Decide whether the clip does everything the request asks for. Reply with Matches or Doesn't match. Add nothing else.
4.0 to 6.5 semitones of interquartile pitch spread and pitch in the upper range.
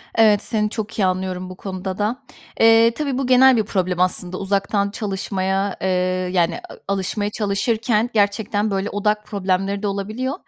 Doesn't match